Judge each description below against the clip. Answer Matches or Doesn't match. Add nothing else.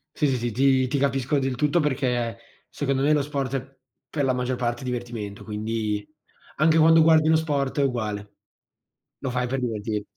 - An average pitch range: Matches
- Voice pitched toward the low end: Matches